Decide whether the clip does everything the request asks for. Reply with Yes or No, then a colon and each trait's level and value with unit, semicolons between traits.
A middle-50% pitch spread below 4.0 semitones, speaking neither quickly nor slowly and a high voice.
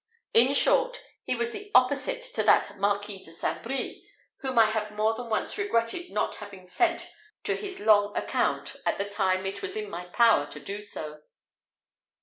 No: average, 5.2 semitones; average, 180 wpm; high, 220 Hz